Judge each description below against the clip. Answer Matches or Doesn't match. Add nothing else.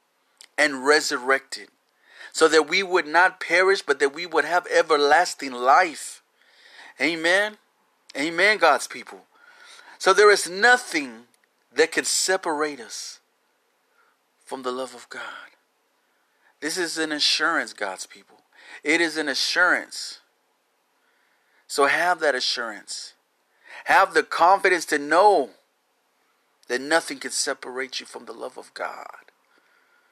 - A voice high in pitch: Matches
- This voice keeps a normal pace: Doesn't match